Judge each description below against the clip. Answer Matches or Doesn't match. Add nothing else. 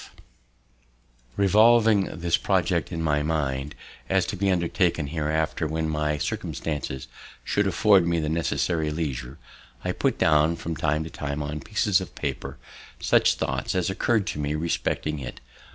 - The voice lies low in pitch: Matches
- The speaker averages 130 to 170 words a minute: Matches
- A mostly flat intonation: Doesn't match